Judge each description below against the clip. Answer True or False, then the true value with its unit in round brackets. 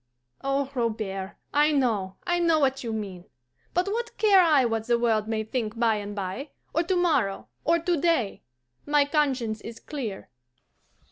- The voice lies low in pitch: False (250 Hz)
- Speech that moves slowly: False (165 wpm)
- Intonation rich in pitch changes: True (6.2 semitones)